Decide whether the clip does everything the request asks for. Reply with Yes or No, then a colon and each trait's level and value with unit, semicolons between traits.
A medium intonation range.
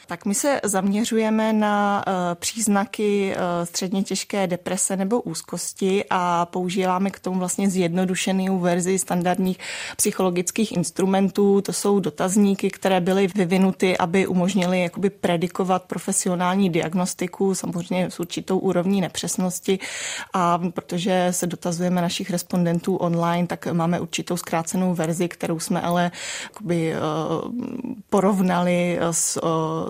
No: narrow, 1.9 semitones